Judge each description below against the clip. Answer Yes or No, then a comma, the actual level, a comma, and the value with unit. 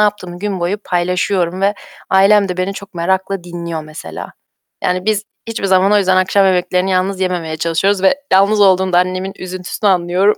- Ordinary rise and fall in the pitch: No, narrow, 1.7 semitones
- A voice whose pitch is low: No, medium, 185 Hz